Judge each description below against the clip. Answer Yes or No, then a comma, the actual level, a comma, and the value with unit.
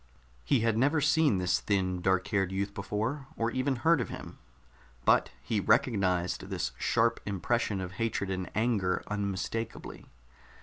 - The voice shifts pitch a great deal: No, average, 4.0 semitones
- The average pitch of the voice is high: No, low, 105 Hz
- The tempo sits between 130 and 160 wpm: Yes, average, 145 wpm